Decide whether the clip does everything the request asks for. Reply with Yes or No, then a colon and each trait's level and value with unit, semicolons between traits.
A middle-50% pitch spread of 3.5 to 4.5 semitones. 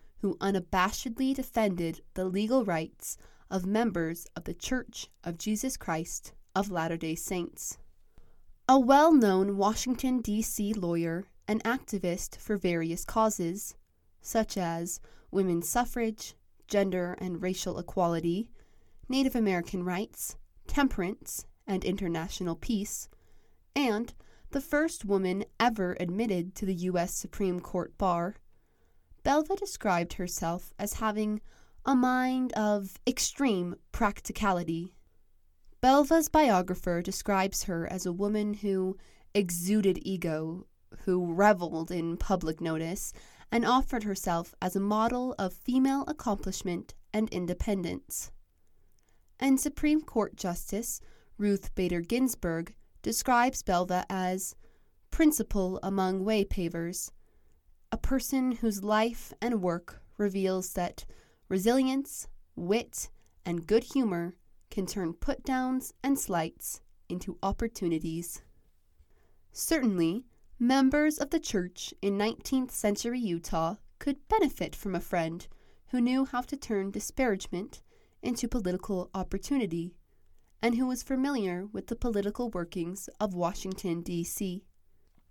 No: average, 5.2 semitones